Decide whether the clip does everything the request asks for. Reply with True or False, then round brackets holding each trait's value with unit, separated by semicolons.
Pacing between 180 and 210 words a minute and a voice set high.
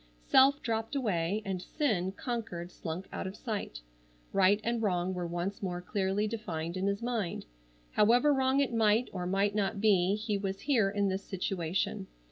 False (170 wpm; 200 Hz)